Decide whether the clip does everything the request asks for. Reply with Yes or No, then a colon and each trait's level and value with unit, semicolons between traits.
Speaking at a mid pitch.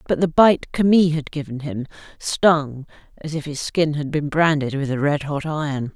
Yes: medium, 150 Hz